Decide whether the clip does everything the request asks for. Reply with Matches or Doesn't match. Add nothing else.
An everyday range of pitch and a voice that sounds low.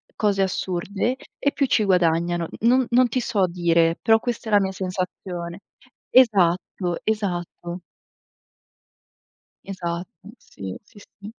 Doesn't match